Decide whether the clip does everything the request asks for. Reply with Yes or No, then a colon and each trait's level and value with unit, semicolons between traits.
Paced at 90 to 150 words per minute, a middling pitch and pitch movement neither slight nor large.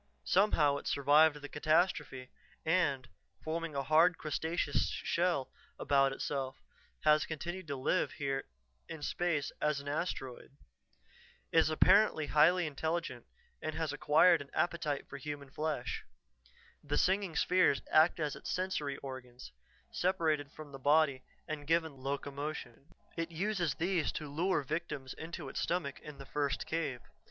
Yes: average, 140 wpm; medium, 150 Hz; average, 3.0 semitones